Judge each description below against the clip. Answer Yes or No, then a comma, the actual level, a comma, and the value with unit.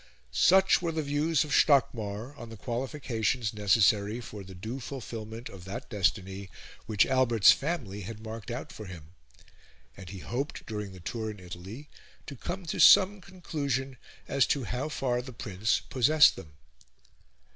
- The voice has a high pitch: No, low, 115 Hz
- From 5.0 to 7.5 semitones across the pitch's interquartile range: Yes, wide, 5.4 semitones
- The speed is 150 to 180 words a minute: Yes, average, 155 wpm